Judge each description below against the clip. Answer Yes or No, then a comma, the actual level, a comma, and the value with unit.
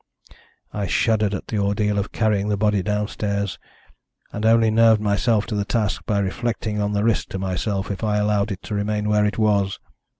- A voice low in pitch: Yes, low, 105 Hz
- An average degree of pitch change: No, narrow, 1.2 semitones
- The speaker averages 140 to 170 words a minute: No, average, 195 wpm